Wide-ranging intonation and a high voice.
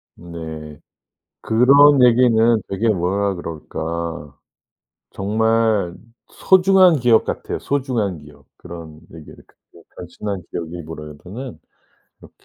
No: wide, 6.0 semitones; low, 100 Hz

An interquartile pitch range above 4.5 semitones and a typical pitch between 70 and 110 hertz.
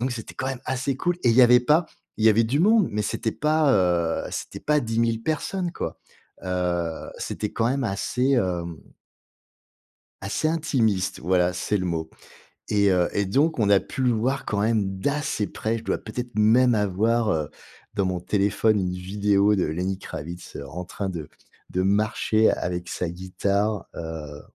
Yes: average, 5.1 semitones; low, 105 Hz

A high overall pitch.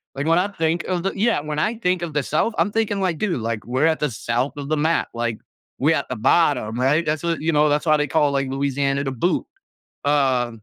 No: medium, 150 Hz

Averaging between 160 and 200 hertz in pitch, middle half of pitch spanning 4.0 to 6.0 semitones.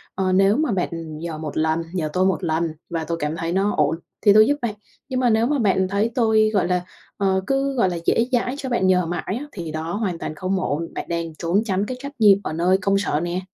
Yes: high, 190 Hz; average, 4.4 semitones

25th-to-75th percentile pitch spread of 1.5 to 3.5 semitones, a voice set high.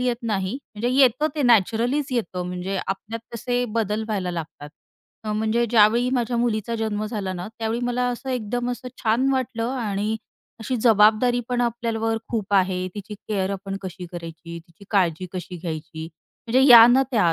No: average, 4.2 semitones; high, 220 Hz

